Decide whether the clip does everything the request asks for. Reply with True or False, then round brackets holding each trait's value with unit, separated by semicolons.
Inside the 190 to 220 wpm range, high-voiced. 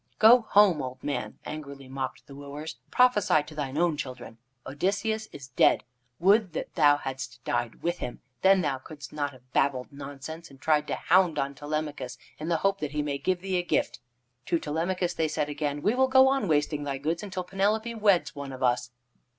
False (200 wpm; 150 Hz)